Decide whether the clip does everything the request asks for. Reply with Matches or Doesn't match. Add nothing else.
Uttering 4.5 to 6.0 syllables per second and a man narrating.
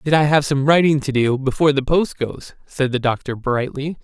Matches